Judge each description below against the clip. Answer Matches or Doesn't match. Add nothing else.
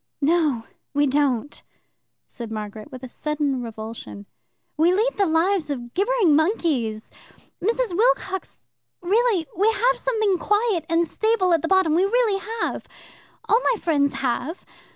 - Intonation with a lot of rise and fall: Matches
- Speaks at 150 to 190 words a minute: Doesn't match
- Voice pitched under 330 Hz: Doesn't match